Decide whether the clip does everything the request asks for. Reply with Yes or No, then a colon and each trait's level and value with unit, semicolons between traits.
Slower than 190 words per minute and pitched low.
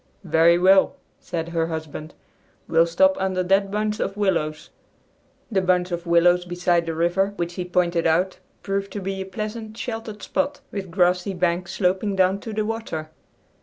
No: average, 165 wpm; medium, 185 Hz